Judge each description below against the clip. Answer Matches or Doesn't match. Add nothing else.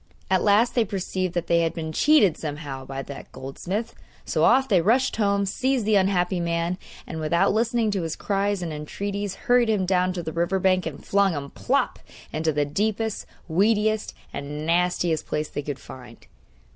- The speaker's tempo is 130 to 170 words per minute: Doesn't match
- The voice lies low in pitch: Doesn't match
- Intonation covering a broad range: Doesn't match